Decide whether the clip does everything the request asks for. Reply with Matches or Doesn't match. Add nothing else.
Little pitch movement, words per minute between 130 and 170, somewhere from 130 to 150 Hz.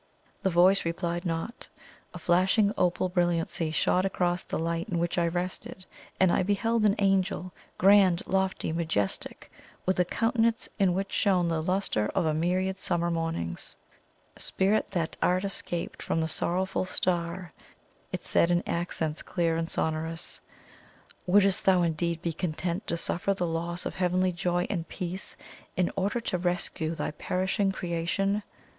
Doesn't match